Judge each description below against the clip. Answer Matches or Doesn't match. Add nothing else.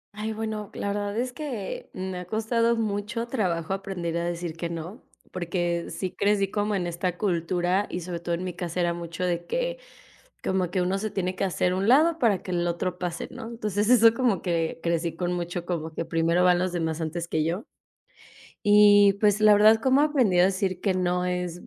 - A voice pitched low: Doesn't match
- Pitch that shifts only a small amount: Doesn't match